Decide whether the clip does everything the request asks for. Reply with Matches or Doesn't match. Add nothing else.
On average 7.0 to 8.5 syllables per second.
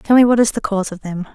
Matches